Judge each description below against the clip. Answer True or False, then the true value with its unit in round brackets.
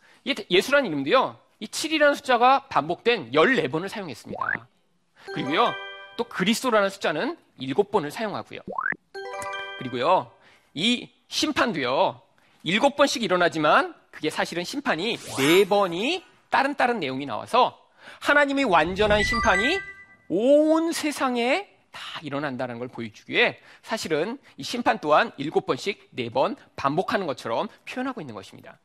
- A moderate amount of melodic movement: False (8.2 semitones)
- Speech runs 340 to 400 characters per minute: False (285 characters per minute)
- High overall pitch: True (235 Hz)